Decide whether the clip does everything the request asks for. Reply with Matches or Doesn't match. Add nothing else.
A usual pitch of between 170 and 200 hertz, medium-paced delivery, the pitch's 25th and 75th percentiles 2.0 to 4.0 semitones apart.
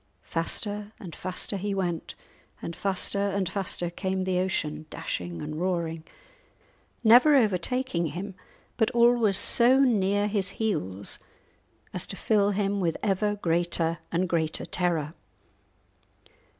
Doesn't match